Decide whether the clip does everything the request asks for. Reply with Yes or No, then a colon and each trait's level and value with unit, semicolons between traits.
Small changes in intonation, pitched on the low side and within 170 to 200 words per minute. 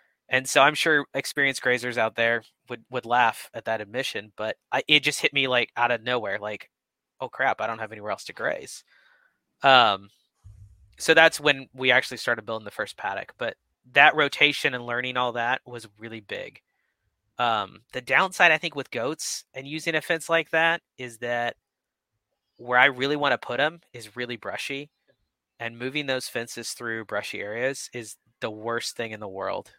No: average, 3.3 semitones; low, 125 Hz; average, 190 wpm